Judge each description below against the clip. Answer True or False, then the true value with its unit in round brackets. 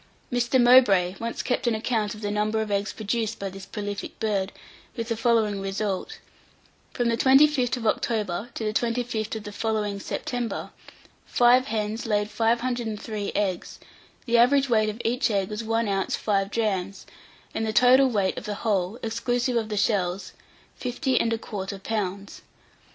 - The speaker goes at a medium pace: True (160 wpm)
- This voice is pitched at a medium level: False (220 Hz)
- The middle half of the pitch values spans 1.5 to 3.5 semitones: True (2.7 semitones)